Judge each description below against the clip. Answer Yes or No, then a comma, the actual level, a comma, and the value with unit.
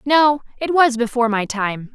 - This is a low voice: No, very high, 250 Hz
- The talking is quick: No, average, 185 wpm